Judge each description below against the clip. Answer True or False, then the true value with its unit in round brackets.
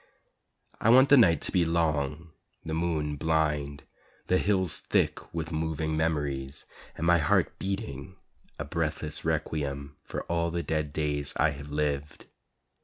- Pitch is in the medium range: False (80 Hz)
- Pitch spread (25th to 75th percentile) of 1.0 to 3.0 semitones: True (2.4 semitones)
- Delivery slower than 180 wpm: True (145 wpm)